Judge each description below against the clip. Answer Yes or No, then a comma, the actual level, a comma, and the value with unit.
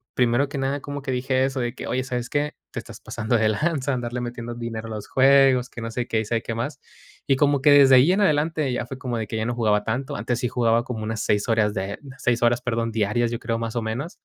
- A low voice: Yes, low, 120 Hz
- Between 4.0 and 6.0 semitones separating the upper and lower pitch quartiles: No, average, 2.8 semitones